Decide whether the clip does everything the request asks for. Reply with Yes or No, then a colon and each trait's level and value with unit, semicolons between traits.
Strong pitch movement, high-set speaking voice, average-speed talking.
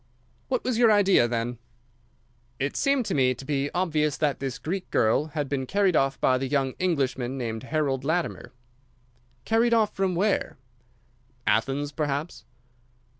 No: wide, 5.9 semitones; medium, 145 Hz; average, 150 wpm